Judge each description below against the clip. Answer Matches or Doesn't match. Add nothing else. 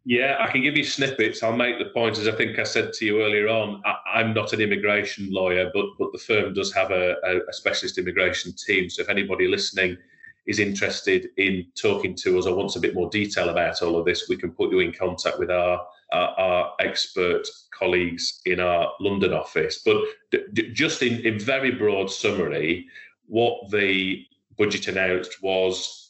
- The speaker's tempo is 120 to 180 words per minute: Doesn't match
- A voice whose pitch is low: Matches